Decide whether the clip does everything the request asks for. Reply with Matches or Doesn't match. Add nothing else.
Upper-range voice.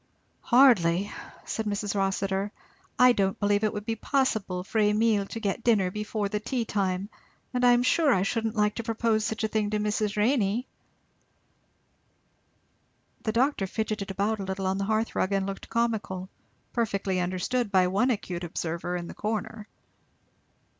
Matches